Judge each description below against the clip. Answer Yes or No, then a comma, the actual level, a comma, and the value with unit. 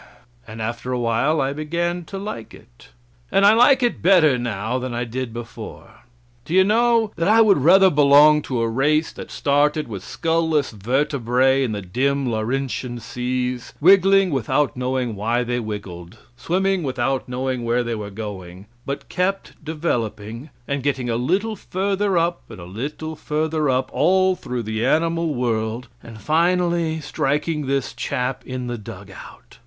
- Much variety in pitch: Yes, wide, 5.8 semitones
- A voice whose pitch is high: No, low, 135 Hz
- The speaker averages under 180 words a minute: Yes, average, 165 wpm